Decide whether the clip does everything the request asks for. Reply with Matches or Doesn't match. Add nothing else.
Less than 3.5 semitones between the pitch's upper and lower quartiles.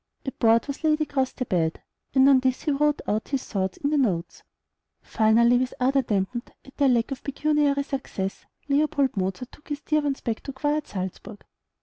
Doesn't match